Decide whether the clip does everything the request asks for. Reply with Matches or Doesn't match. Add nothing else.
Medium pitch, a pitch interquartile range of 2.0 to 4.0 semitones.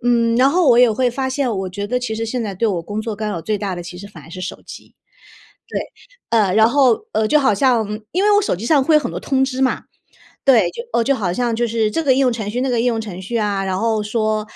Doesn't match